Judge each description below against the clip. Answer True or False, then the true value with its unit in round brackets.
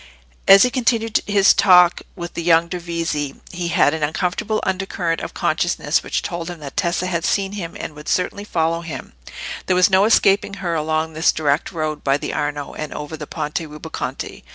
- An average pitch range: True (3.4 semitones)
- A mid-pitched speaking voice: True (170 Hz)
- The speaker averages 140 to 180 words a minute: False (190 wpm)